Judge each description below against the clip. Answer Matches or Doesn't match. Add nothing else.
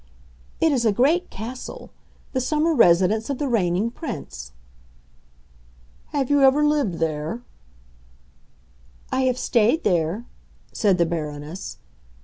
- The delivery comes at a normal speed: Doesn't match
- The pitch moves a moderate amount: Doesn't match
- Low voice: Doesn't match